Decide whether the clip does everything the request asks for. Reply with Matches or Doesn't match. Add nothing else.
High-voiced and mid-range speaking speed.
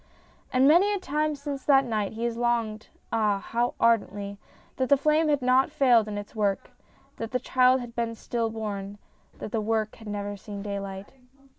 Matches